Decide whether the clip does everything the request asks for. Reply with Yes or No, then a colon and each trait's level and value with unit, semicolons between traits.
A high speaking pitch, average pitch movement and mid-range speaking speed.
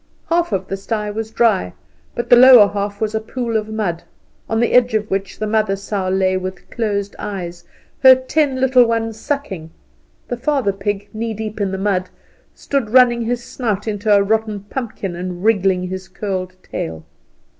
Yes: high, 210 Hz; average, 3.3 semitones; average, 180 wpm